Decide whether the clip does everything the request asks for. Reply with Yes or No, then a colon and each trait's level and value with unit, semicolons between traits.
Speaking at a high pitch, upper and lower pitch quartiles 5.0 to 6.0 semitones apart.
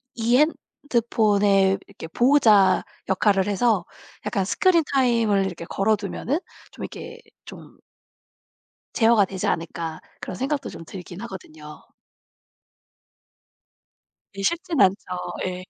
No: high, 205 Hz; average, 4.3 semitones